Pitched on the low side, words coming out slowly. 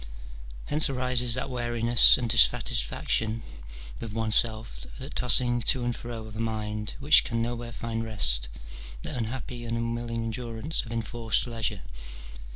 No: low, 115 Hz; average, 150 wpm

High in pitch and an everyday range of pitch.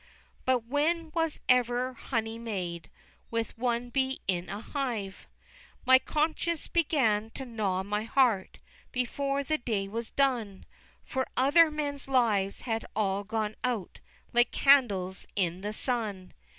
Yes: high, 235 Hz; average, 4.6 semitones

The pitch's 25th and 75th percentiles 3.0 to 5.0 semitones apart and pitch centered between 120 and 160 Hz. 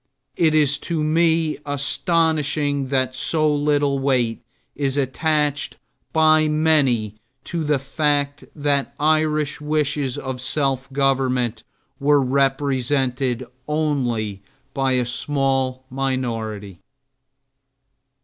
No: narrow, 2.6 semitones; medium, 140 Hz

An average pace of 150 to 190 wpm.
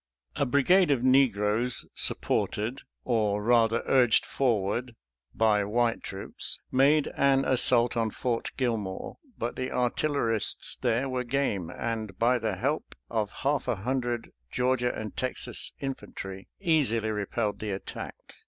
No: average, 140 wpm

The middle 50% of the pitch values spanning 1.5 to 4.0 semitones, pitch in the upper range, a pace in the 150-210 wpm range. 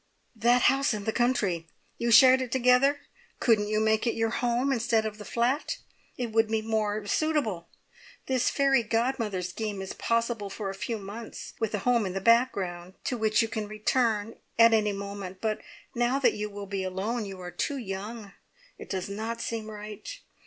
Yes: average, 2.8 semitones; high, 220 Hz; average, 190 wpm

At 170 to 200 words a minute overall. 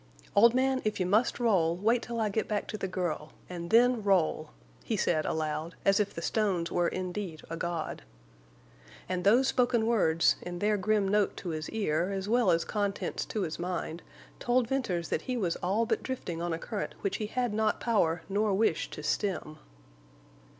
Yes: average, 190 wpm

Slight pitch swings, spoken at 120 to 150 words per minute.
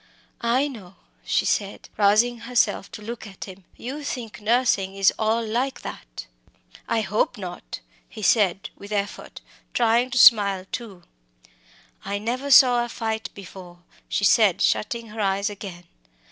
No: average, 3.2 semitones; average, 145 wpm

